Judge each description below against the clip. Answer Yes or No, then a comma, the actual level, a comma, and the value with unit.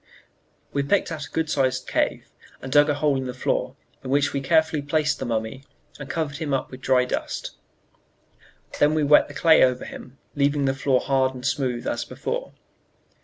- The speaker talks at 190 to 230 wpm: Yes, average, 195 wpm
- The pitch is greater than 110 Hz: Yes, medium, 140 Hz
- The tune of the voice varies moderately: No, narrow, 2.3 semitones